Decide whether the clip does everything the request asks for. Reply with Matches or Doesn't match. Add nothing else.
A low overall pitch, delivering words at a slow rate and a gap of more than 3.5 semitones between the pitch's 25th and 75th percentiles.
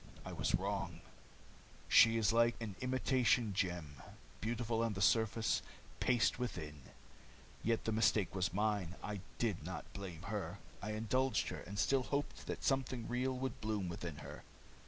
Doesn't match